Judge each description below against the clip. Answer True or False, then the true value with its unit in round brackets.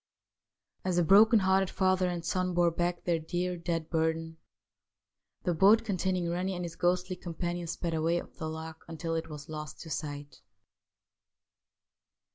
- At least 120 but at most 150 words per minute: False (160 wpm)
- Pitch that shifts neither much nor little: False (2.1 semitones)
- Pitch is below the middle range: False (175 Hz)